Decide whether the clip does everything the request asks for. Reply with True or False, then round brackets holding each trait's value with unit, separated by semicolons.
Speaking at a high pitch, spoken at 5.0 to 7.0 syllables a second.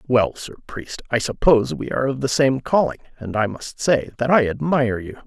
False (125 Hz; 5.5 syllables/s)